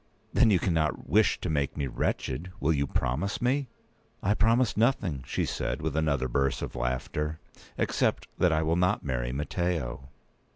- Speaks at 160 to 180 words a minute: Yes, average, 165 wpm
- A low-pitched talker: Yes, very low, 80 Hz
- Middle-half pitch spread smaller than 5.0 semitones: No, average, 5.3 semitones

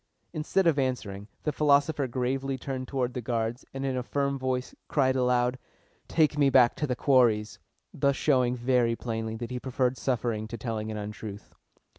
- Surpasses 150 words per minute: Yes, average, 175 wpm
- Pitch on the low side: Yes, low, 125 Hz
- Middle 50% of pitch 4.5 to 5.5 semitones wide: No, narrow, 2.6 semitones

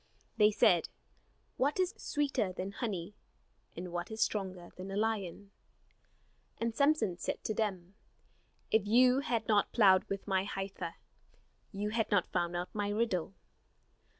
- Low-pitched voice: No, high, 205 Hz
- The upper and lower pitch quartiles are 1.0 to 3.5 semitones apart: Yes, average, 3.2 semitones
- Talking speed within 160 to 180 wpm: No, average, 145 wpm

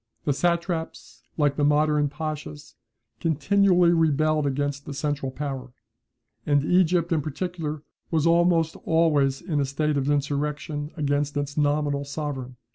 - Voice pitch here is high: No, medium, 150 Hz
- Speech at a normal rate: No, slow, 130 wpm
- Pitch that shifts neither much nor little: No, narrow, 2.3 semitones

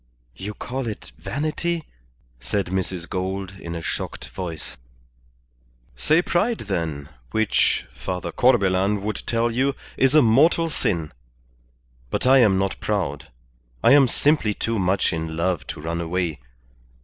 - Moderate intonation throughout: No, wide, 7.1 semitones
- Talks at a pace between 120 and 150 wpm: Yes, slow, 135 wpm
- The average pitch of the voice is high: No, very low, 95 Hz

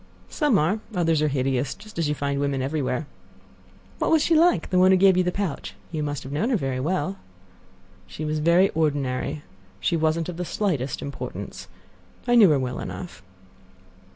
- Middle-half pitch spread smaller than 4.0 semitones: No, average, 4.9 semitones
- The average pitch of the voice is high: No, medium, 160 Hz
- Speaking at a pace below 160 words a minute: No, average, 180 wpm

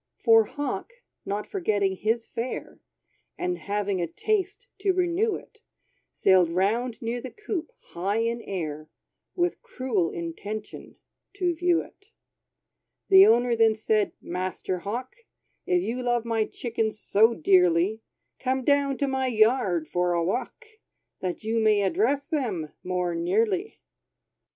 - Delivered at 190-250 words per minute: No, slow, 135 wpm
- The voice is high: Yes, high, 225 Hz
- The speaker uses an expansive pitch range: Yes, wide, 6.7 semitones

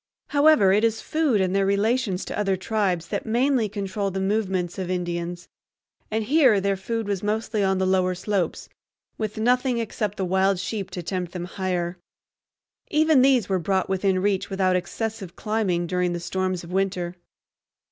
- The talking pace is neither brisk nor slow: Yes, average, 170 wpm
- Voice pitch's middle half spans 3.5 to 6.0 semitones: No, average, 3.1 semitones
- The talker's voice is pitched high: Yes, high, 195 Hz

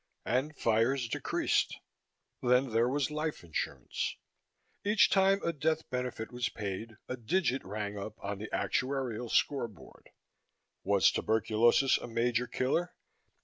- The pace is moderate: No, slow, 125 wpm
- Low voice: Yes, low, 125 Hz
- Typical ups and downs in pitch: Yes, average, 3.9 semitones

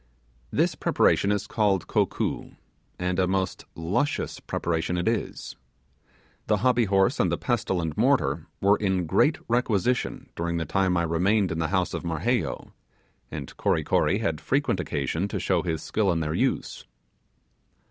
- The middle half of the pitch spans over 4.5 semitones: No, average, 3.8 semitones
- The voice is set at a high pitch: No, very low, 95 Hz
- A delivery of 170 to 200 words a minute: No, average, 155 wpm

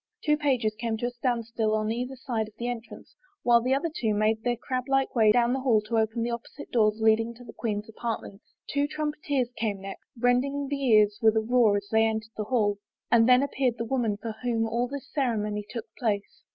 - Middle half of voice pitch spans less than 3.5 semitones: Yes, narrow, 2.5 semitones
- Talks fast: Yes, fast, 225 wpm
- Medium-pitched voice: No, high, 230 Hz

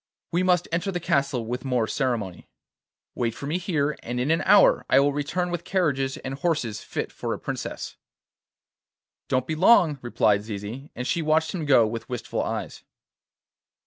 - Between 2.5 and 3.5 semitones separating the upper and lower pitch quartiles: No, average, 5.3 semitones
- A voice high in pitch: No, medium, 140 Hz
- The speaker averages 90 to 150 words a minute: No, average, 175 wpm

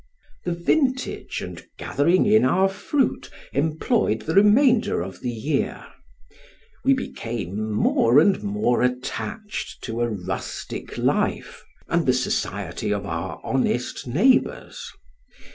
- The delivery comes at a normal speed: No, slow, 115 wpm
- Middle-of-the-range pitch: Yes, medium, 145 Hz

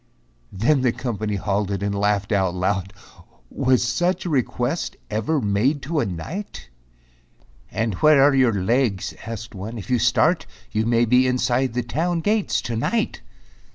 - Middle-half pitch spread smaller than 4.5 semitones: No, average, 5.0 semitones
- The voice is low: Yes, low, 120 Hz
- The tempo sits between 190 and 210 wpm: No, average, 155 wpm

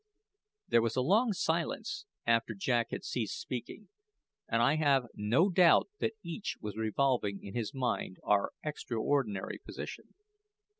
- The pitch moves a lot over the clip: Yes, wide, 6.6 semitones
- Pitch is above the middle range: No, low, 125 Hz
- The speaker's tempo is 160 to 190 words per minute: No, average, 140 wpm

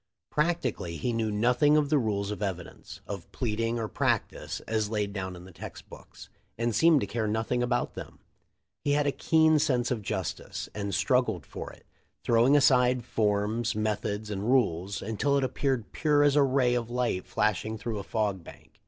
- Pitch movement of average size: Yes, average, 3.9 semitones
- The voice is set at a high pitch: No, low, 115 Hz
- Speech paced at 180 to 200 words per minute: Yes, average, 190 wpm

